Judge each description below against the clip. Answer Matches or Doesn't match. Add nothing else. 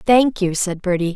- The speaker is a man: Doesn't match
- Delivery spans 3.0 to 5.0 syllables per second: Matches